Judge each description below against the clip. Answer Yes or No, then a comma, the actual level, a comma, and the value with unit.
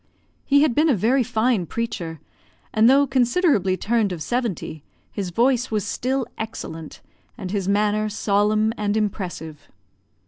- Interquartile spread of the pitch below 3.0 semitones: No, average, 4.2 semitones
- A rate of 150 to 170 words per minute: No, average, 140 wpm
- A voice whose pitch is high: Yes, high, 215 Hz